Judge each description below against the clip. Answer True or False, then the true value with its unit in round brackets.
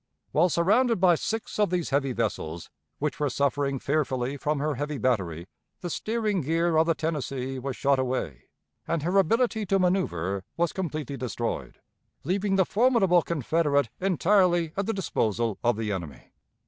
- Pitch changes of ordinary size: False (6.1 semitones)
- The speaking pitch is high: False (155 Hz)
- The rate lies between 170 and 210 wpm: False (160 wpm)